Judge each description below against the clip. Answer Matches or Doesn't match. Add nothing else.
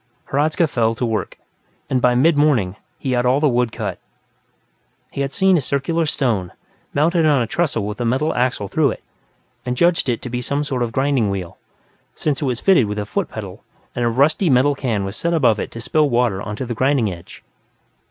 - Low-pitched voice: Matches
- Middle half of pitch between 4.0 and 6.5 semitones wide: Matches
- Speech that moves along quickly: Matches